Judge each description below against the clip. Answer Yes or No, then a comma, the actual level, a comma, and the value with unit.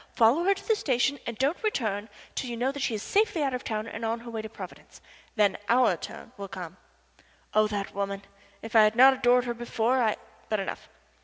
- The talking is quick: Yes, fast, 220 wpm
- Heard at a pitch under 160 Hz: No, high, 230 Hz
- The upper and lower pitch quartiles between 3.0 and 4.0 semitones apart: Yes, average, 3.5 semitones